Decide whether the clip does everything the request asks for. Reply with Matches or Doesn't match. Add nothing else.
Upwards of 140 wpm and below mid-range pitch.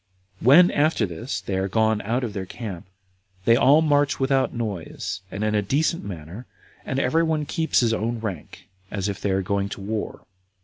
Matches